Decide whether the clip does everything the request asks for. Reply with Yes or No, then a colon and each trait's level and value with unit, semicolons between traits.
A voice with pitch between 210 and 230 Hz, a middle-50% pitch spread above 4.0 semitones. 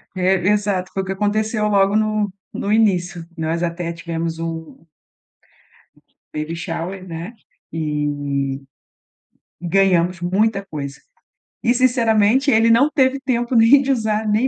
No: high, 195 Hz; average, 4.7 semitones